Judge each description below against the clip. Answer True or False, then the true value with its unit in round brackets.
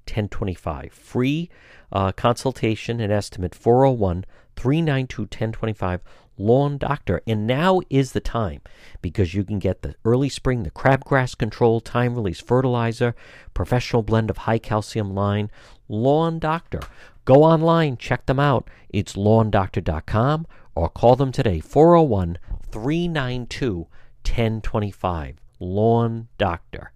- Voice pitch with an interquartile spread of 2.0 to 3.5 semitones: False (4.7 semitones)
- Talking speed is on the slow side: True (110 wpm)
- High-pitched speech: False (115 Hz)